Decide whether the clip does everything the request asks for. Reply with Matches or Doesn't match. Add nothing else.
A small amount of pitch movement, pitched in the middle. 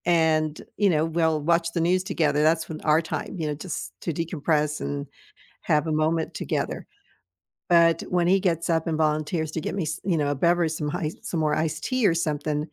Matches